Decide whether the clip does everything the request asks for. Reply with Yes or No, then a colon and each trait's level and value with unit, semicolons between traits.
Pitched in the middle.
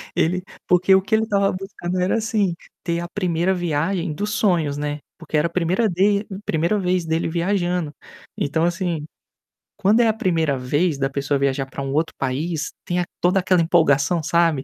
Yes: medium, 175 Hz